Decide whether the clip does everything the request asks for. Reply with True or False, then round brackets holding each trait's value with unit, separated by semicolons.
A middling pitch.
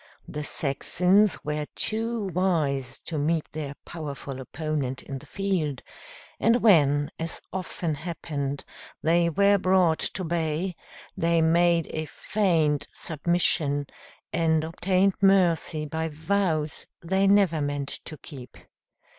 True (160 Hz)